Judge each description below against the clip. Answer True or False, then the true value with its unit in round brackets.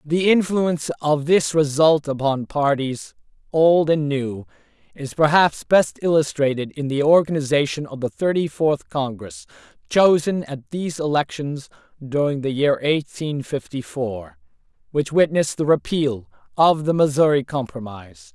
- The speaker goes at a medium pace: False (130 wpm)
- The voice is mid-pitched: True (145 Hz)